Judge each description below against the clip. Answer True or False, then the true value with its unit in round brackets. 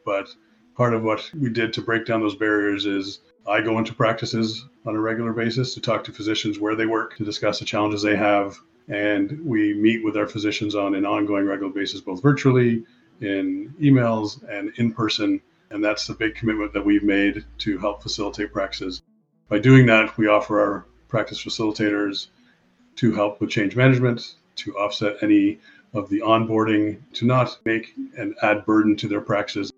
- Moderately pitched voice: False (110 Hz)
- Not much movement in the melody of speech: True (2.0 semitones)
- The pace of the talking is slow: False (185 wpm)